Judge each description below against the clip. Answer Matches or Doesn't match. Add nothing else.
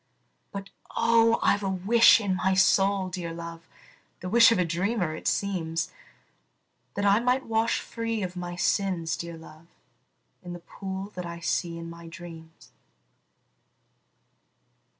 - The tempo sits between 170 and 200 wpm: Doesn't match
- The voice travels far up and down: Doesn't match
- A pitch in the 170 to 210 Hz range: Matches